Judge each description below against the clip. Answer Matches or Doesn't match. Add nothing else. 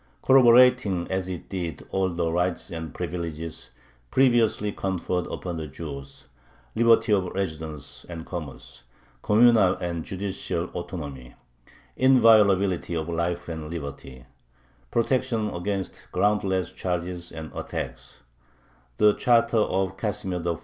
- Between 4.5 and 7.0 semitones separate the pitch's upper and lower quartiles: Doesn't match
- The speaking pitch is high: Doesn't match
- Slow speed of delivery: Matches